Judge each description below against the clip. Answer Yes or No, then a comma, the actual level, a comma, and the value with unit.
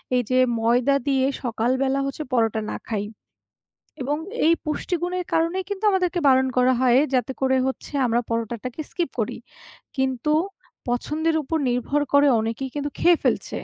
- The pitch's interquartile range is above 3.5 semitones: Yes, average, 4.1 semitones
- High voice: Yes, very high, 265 Hz